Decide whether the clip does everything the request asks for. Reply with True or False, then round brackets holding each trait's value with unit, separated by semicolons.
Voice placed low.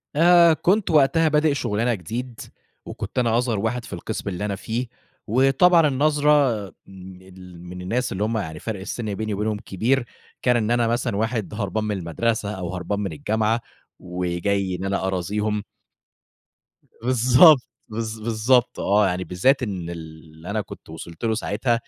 True (110 Hz)